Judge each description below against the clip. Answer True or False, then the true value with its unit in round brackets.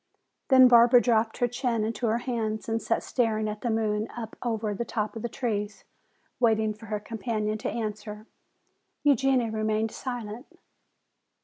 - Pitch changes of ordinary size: False (1.8 semitones)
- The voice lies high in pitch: True (225 Hz)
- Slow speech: False (155 wpm)